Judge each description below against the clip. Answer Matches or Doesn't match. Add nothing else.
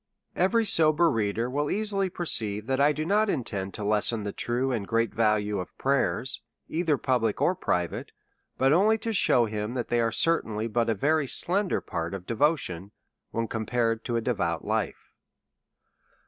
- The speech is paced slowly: Doesn't match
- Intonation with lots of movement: Matches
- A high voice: Doesn't match